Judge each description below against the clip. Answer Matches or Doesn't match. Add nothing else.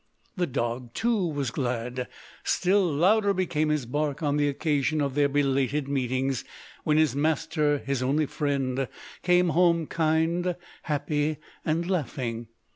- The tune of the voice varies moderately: Matches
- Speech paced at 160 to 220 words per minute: Doesn't match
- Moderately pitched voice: Matches